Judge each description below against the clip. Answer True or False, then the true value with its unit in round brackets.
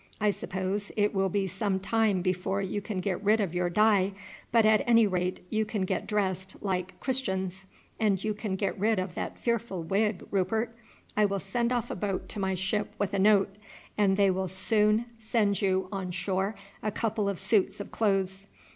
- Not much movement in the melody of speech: True (2.0 semitones)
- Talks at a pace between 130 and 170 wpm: False (195 wpm)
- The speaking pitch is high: True (200 Hz)